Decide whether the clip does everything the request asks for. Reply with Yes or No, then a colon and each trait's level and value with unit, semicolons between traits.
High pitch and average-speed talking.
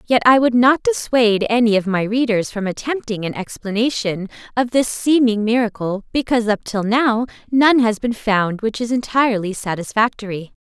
Yes: high, 225 Hz; average, 165 wpm